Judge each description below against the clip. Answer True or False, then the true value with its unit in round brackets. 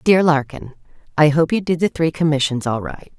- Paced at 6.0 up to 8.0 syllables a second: False (5.2 syllables/s)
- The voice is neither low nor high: True (155 Hz)